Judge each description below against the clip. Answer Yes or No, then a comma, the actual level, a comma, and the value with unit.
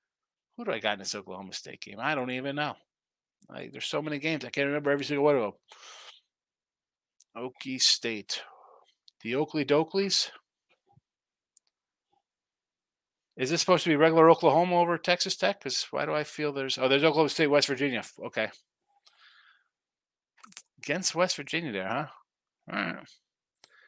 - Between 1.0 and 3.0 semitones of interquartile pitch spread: No, average, 3.6 semitones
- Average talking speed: Yes, average, 155 wpm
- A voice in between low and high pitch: Yes, medium, 150 Hz